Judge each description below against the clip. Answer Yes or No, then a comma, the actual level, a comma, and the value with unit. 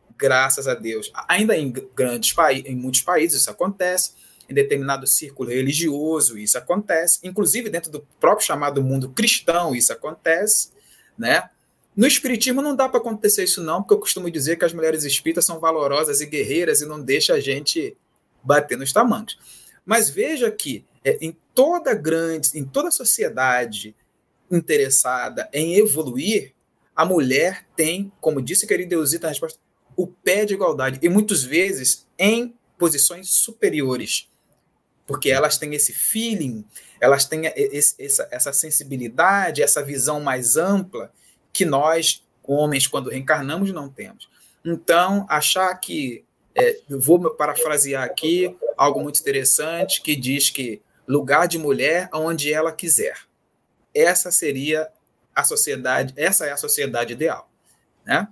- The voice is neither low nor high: Yes, medium, 160 Hz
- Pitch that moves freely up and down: Yes, wide, 6.4 semitones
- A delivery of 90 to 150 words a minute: Yes, average, 140 wpm